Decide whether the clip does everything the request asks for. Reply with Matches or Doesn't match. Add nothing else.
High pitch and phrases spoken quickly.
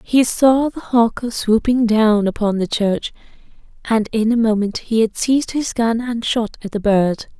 Doesn't match